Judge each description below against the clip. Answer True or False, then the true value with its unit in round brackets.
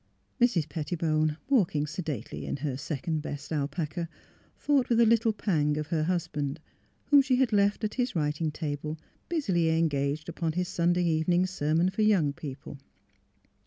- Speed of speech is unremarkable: True (155 wpm)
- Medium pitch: True (165 Hz)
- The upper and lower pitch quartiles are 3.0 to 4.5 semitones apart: True (4.0 semitones)